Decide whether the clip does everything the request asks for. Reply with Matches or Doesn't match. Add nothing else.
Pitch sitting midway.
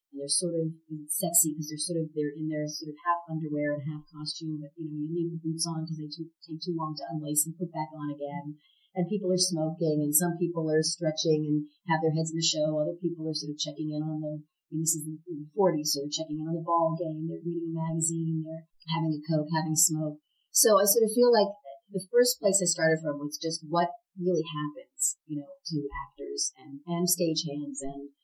Matches